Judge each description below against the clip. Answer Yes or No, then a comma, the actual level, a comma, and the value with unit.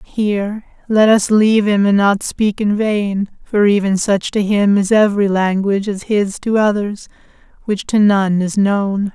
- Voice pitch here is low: No, high, 205 Hz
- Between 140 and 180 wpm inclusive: Yes, average, 175 wpm